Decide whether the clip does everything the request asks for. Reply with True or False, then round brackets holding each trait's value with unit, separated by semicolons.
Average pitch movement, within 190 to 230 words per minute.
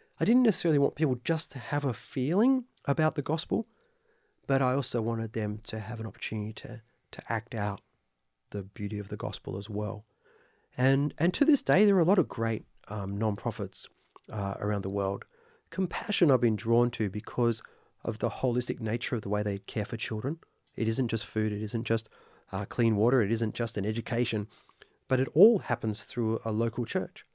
True (4.5 semitones; 195 wpm)